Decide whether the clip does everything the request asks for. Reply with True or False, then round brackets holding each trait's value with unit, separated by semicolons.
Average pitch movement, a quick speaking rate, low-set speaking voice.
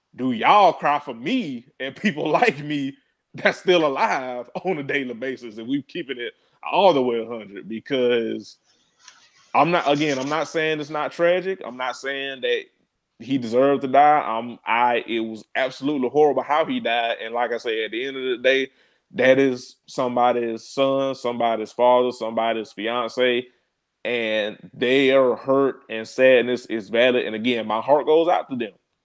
False (4.3 semitones; 175 wpm; 130 Hz)